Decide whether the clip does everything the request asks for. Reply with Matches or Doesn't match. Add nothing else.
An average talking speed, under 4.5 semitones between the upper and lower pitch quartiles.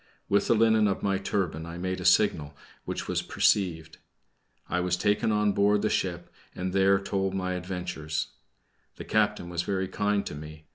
Matches